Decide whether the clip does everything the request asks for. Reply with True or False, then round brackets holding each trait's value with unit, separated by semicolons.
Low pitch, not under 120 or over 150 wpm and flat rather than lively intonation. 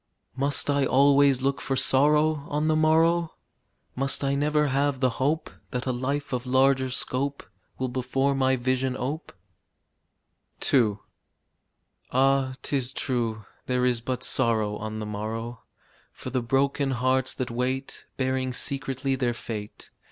True (130 Hz; 140 wpm; 1.9 semitones)